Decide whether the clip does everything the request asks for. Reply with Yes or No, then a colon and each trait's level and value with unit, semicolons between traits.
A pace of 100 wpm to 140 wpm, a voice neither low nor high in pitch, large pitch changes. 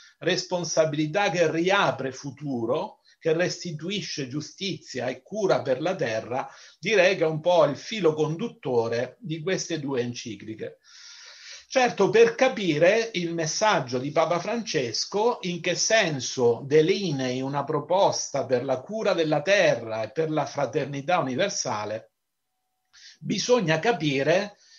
Yes: average, 120 wpm; medium, 165 Hz; wide, 6.1 semitones